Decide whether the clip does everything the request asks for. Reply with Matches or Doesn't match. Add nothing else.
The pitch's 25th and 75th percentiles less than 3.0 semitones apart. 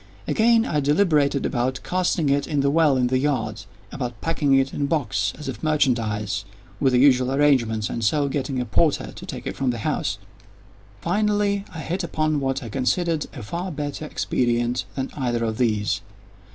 Doesn't match